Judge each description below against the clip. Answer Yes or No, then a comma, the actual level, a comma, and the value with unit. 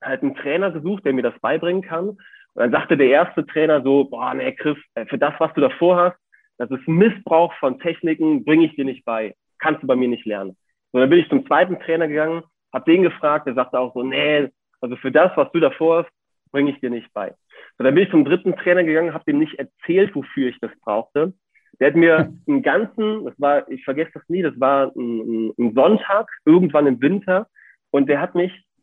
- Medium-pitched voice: Yes, medium, 160 Hz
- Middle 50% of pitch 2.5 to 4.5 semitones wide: No, average, 4.9 semitones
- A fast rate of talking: Yes, fast, 225 wpm